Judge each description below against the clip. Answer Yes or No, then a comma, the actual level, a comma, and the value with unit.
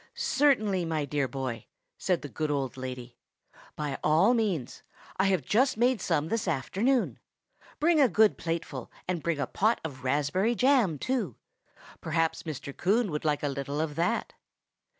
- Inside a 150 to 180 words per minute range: Yes, average, 160 wpm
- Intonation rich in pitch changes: Yes, wide, 7.3 semitones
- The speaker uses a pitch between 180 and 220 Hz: No, medium, 165 Hz